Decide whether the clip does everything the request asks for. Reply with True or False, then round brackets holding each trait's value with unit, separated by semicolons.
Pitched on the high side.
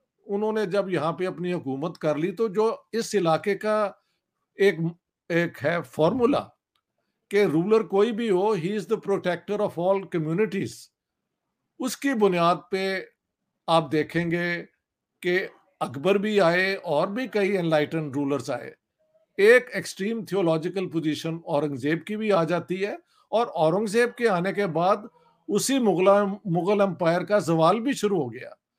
True (195 Hz)